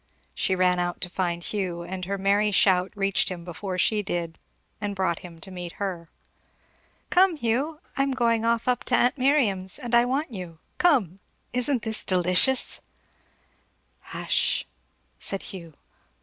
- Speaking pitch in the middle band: No, high, 195 Hz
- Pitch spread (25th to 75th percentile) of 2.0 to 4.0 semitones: No, average, 5.0 semitones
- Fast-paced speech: No, average, 155 wpm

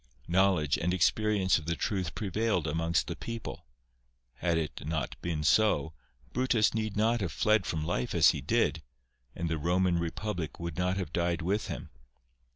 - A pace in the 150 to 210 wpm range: Yes, average, 165 wpm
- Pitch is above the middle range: No, very low, 90 Hz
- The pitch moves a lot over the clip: No, average, 4.4 semitones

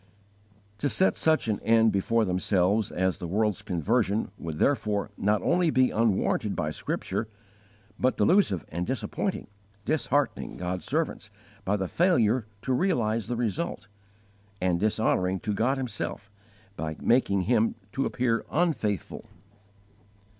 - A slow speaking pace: Yes, slow, 130 wpm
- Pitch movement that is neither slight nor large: Yes, average, 5.0 semitones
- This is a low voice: Yes, low, 110 Hz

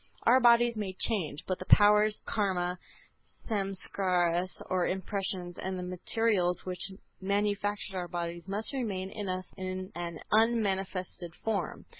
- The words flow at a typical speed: No, slow, 130 wpm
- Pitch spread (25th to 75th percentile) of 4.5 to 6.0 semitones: No, narrow, 2.6 semitones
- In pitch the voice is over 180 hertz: Yes, high, 190 Hz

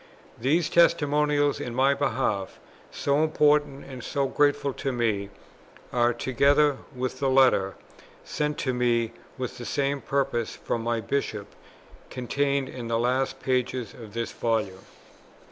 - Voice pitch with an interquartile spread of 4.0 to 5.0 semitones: No, average, 3.3 semitones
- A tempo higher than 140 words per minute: No, slow, 135 wpm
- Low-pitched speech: Yes, low, 130 Hz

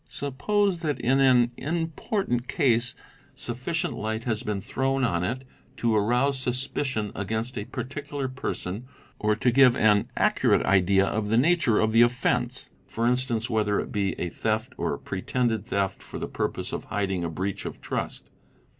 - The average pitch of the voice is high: No, low, 120 Hz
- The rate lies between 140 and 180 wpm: Yes, average, 165 wpm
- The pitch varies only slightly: No, average, 3.9 semitones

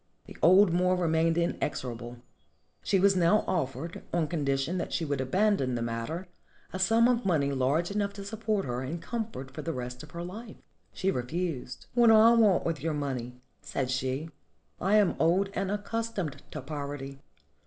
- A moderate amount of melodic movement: No, wide, 6.5 semitones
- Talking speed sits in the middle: Yes, average, 180 wpm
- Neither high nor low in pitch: Yes, medium, 165 Hz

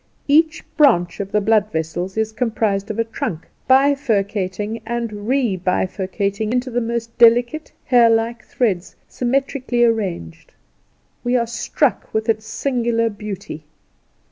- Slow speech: Yes, slow, 125 wpm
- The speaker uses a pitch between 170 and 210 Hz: No, high, 225 Hz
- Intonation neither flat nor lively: Yes, average, 3.3 semitones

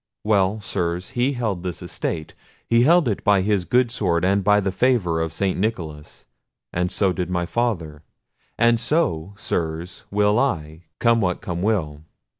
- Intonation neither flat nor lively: Yes, average, 4.8 semitones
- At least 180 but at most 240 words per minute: No, average, 155 wpm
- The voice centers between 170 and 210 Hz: No, very low, 95 Hz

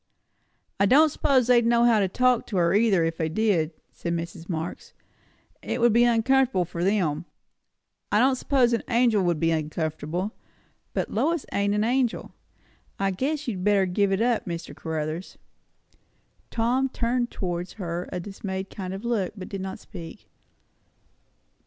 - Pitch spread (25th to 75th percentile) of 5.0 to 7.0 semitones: Yes, wide, 5.4 semitones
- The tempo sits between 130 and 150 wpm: No, average, 160 wpm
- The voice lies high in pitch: Yes, high, 200 Hz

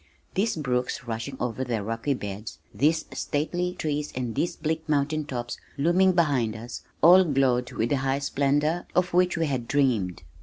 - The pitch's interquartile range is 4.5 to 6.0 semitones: Yes, average, 4.8 semitones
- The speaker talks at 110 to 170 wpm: Yes, average, 165 wpm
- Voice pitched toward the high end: No, medium, 140 Hz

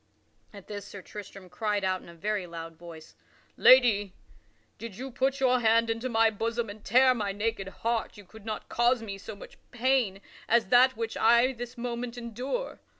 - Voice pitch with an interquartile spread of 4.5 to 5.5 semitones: No, average, 3.3 semitones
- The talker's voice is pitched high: Yes, high, 225 Hz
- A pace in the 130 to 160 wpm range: No, average, 185 wpm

